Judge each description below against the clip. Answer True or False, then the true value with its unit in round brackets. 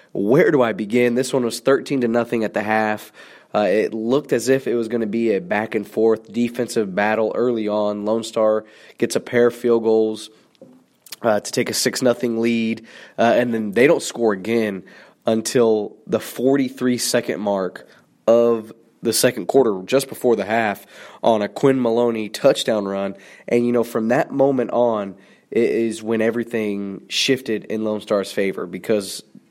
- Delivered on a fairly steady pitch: True (1.8 semitones)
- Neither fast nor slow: True (185 wpm)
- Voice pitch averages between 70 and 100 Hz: False (115 Hz)